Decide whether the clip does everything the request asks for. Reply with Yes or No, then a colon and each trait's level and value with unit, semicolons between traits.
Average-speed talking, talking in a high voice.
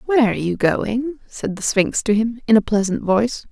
No: fast, 220 wpm; high, 225 Hz